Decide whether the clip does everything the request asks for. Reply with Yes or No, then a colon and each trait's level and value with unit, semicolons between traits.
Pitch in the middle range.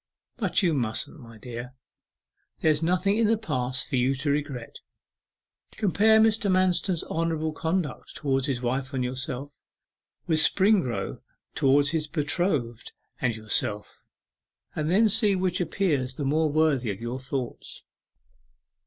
Yes: medium, 150 Hz